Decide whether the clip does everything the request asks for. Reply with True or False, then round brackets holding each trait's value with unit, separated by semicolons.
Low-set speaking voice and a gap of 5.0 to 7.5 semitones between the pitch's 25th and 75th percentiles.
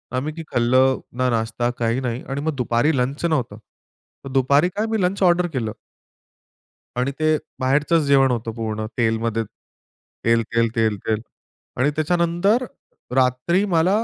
True (130 Hz; 5.6 semitones)